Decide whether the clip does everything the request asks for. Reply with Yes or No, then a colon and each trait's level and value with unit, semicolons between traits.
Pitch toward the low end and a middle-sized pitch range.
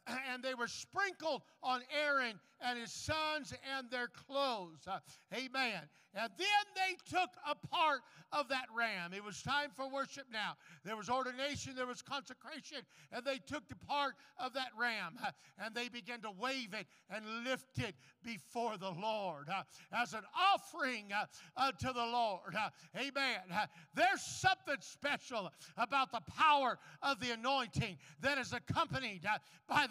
No: very high, 250 Hz; average, 4.5 semitones